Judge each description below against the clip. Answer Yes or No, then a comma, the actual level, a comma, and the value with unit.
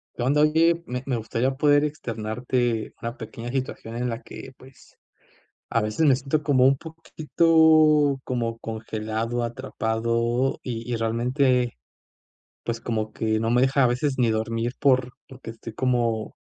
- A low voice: Yes, low, 125 Hz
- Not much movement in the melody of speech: No, average, 3.0 semitones